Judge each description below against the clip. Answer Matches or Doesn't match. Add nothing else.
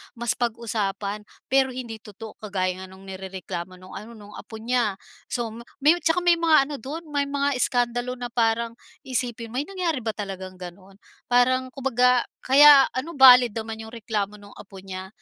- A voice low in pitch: Doesn't match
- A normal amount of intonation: Matches